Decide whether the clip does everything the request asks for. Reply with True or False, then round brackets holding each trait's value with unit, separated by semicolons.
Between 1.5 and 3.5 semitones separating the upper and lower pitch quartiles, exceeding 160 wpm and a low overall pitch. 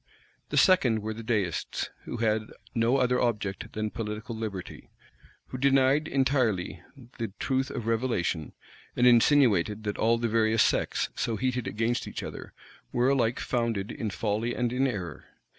False (2.8 semitones; 155 wpm; 115 Hz)